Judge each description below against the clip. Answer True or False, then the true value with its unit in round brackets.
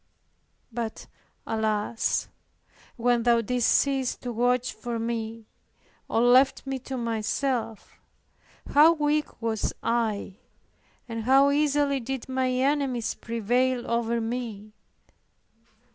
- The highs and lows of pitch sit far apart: False (2.7 semitones)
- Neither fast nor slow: False (105 wpm)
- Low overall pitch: False (240 Hz)